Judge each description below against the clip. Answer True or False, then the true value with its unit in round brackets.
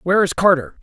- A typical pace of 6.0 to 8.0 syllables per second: True (6.4 syllables/s)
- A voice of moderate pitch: True (170 Hz)